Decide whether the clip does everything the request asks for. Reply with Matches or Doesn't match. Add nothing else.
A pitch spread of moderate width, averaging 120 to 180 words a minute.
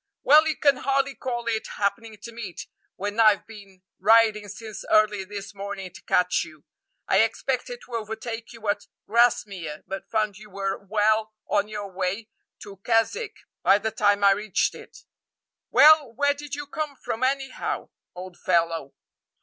Matches